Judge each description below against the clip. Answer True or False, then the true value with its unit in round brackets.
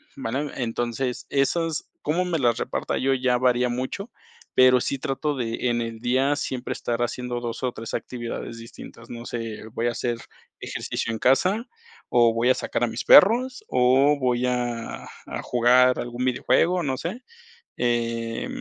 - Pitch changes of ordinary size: False (2.3 semitones)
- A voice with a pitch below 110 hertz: False (125 Hz)